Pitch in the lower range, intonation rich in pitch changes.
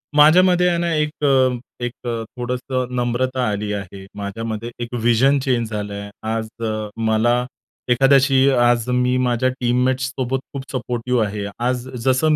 No: low, 125 Hz; narrow, 2.6 semitones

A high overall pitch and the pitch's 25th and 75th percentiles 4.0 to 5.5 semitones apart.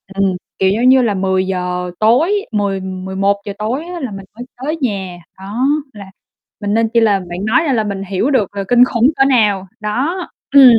Yes: high, 210 Hz; average, 4.5 semitones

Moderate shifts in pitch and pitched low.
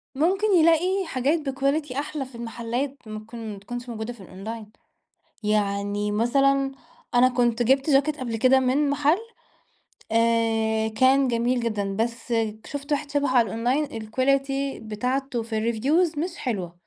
No: average, 3.8 semitones; very high, 250 Hz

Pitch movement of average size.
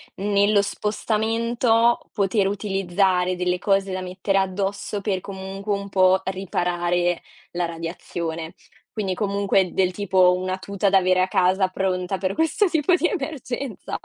No: narrow, 1.9 semitones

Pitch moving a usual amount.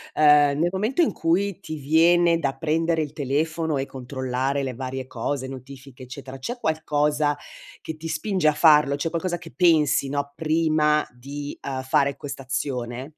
Yes: average, 3.0 semitones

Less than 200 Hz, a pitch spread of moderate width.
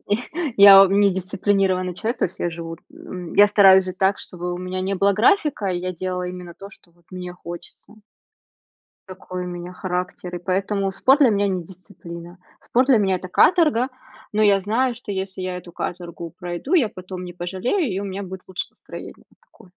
No: medium, 185 Hz; narrow, 2.1 semitones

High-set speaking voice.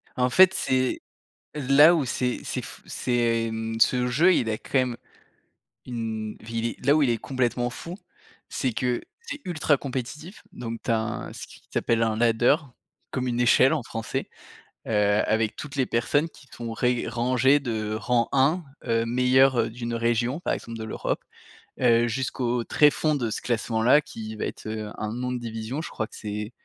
No: low, 120 Hz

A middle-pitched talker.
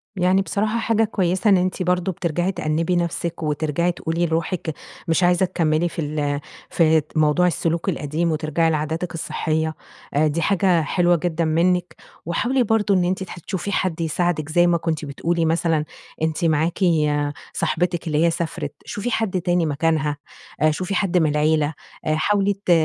Yes: medium, 170 Hz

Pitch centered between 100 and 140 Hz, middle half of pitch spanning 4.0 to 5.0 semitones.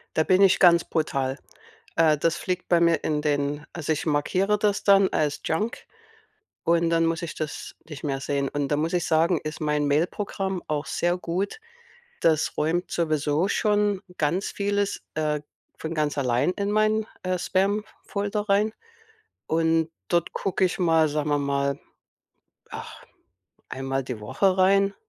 No: medium, 165 Hz; average, 4.3 semitones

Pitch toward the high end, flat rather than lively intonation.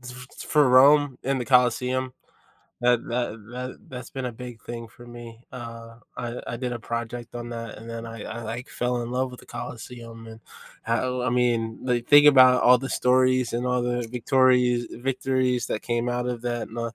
No: low, 120 Hz; narrow, 1.4 semitones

